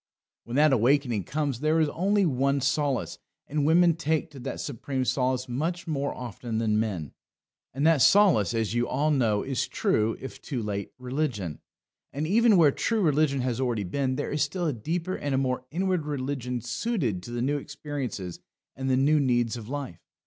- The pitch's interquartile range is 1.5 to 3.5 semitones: No, average, 4.2 semitones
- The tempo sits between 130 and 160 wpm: No, average, 185 wpm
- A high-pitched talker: No, low, 135 Hz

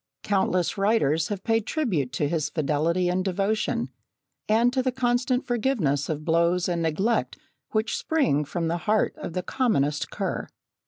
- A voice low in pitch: No, medium, 185 Hz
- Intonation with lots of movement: Yes, wide, 5.9 semitones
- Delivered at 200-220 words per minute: No, average, 155 wpm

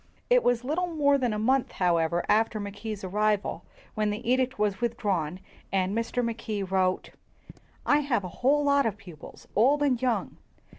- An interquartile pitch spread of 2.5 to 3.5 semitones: No, average, 4.6 semitones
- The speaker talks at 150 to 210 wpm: Yes, average, 165 wpm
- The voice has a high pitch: Yes, high, 225 Hz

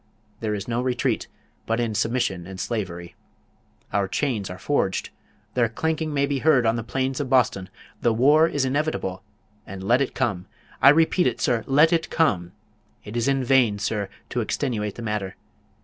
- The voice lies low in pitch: Yes, low, 120 Hz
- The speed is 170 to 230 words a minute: Yes, average, 180 wpm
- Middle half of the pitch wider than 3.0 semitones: Yes, average, 5.1 semitones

